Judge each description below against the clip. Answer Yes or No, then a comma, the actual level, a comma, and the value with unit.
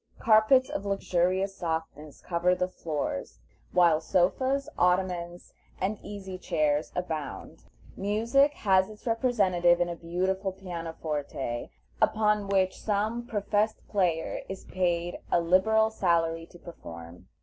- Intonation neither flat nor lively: Yes, average, 3.5 semitones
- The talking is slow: Yes, slow, 115 wpm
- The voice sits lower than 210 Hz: Yes, medium, 185 Hz